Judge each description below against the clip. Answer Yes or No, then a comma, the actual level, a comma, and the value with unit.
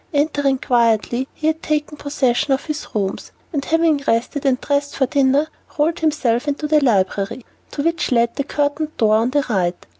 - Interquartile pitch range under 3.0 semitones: No, average, 3.9 semitones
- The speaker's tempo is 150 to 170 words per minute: No, average, 180 wpm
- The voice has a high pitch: Yes, very high, 280 Hz